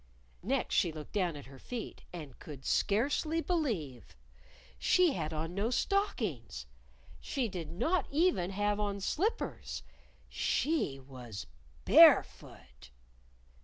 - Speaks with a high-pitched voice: Yes, high, 195 Hz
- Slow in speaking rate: Yes, slow, 115 wpm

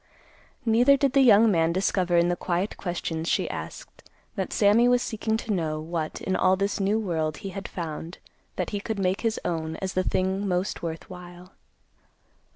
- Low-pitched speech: No, medium, 185 Hz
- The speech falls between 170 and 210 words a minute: Yes, average, 185 wpm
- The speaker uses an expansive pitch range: No, average, 3.5 semitones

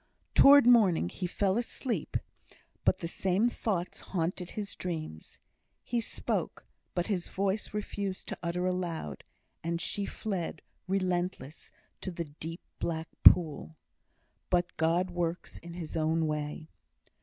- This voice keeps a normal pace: No, slow, 130 wpm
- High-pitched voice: No, medium, 175 Hz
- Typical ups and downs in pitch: Yes, average, 3.0 semitones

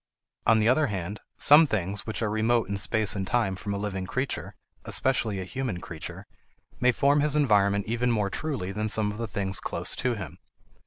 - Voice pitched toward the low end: Yes, low, 110 Hz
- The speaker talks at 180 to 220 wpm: Yes, average, 200 wpm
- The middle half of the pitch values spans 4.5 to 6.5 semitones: No, average, 3.9 semitones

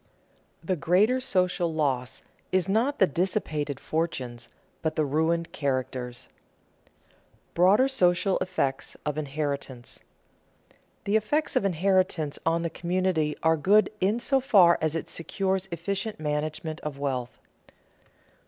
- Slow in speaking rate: Yes, slow, 125 wpm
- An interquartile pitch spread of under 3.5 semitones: No, average, 4.4 semitones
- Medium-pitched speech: Yes, medium, 170 Hz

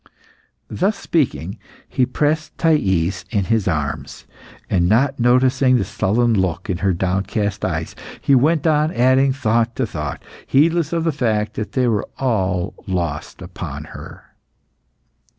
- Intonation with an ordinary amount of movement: No, wide, 6.4 semitones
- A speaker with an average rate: Yes, average, 145 wpm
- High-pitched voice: No, low, 115 Hz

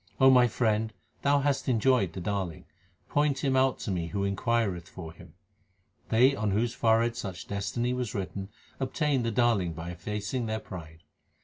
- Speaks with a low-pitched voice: Yes, low, 110 Hz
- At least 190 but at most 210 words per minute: No, average, 170 wpm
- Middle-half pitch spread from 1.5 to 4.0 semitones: No, average, 4.7 semitones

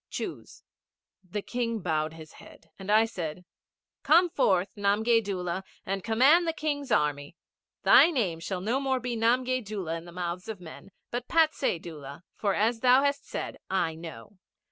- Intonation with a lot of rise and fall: Yes, wide, 6.3 semitones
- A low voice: No, high, 205 Hz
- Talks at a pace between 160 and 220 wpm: Yes, average, 165 wpm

